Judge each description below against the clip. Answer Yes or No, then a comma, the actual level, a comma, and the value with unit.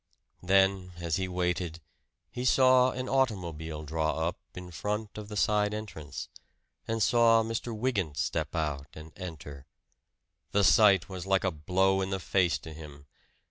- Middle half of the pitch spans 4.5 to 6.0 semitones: Yes, average, 4.8 semitones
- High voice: No, very low, 95 Hz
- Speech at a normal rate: Yes, average, 155 wpm